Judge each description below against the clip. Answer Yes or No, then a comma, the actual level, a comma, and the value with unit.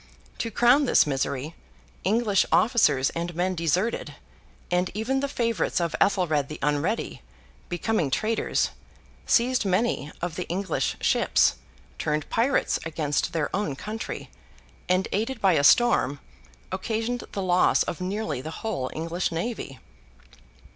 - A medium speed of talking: No, slow, 130 wpm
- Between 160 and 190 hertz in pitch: Yes, medium, 185 Hz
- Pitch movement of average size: No, wide, 6.0 semitones